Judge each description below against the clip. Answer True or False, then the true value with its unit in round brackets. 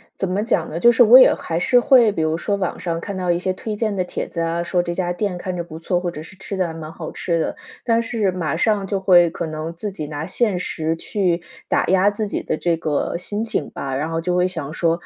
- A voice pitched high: False (180 Hz)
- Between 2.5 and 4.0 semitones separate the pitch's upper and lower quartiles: True (3.4 semitones)